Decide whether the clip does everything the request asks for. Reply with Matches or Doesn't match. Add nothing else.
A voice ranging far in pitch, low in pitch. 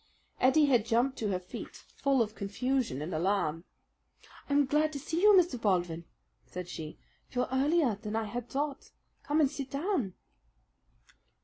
Doesn't match